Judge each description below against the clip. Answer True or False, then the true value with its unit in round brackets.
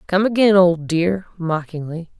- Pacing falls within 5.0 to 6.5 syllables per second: False (4.2 syllables/s)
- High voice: False (180 Hz)